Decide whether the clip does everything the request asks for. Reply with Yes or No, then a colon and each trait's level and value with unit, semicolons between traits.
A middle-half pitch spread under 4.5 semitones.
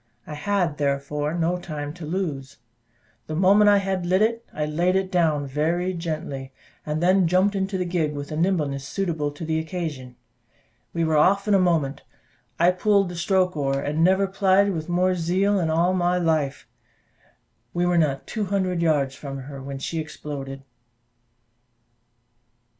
Yes: average, 3.9 semitones